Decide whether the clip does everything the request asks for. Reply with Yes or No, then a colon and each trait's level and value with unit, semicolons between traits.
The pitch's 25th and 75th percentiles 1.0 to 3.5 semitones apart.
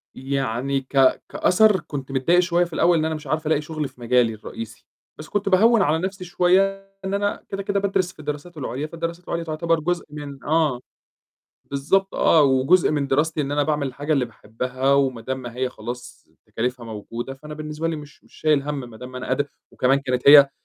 No: average, 4.3 semitones